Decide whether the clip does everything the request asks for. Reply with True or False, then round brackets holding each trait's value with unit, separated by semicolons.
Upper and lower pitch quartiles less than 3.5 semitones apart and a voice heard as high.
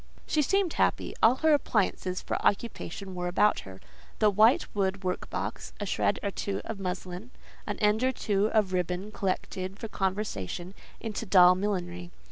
True (3.0 semitones; 195 Hz)